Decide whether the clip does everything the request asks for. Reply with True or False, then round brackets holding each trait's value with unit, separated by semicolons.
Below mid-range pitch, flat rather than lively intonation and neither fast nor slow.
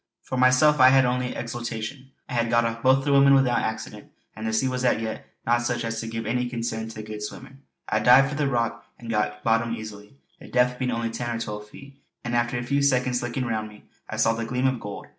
False (120 Hz; 2.2 semitones; 250 wpm)